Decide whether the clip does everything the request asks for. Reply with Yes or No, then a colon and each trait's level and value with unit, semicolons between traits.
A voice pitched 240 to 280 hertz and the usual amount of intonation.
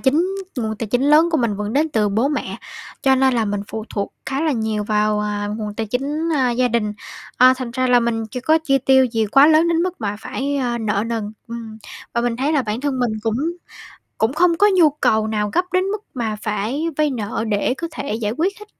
Yes: high, 245 Hz; average, 4.9 semitones